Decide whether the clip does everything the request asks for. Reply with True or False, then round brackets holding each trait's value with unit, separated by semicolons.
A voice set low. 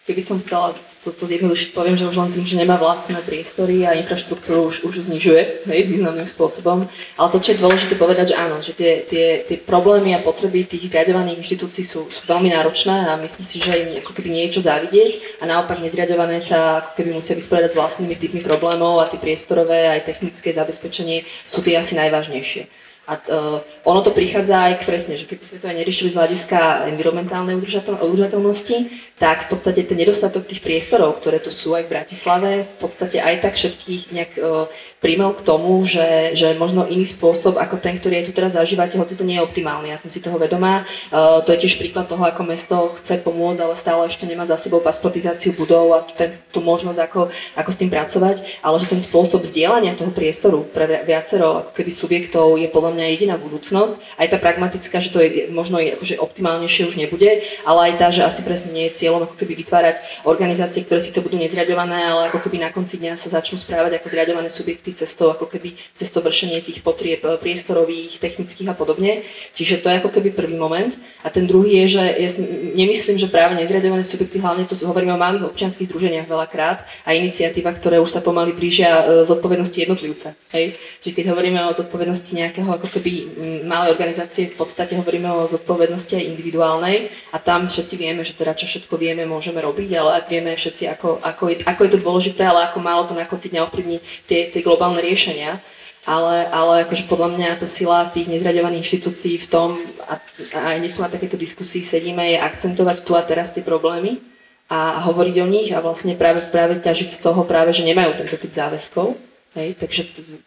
False (175 Hz)